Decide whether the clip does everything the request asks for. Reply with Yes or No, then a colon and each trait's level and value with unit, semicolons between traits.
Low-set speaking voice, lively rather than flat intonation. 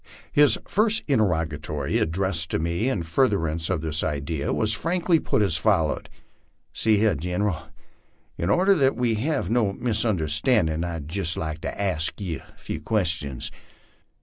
Yes: very low, 90 Hz; wide, 5.8 semitones